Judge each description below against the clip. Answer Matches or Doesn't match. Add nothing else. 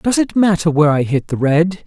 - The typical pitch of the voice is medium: Matches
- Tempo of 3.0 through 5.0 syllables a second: Doesn't match